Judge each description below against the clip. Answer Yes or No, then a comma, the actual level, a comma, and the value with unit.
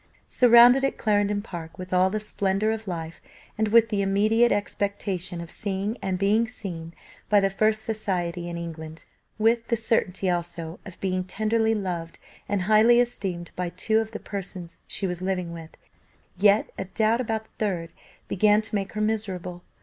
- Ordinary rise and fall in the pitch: Yes, average, 3.5 semitones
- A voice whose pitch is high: Yes, high, 200 Hz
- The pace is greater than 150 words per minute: Yes, average, 170 wpm